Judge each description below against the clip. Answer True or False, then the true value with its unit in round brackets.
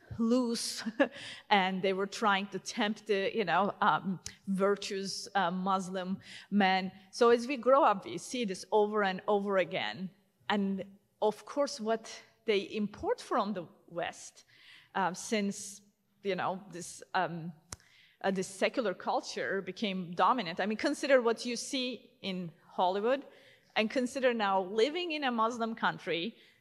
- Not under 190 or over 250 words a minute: False (145 wpm)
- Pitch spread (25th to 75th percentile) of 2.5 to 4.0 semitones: True (3.7 semitones)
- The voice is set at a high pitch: True (205 Hz)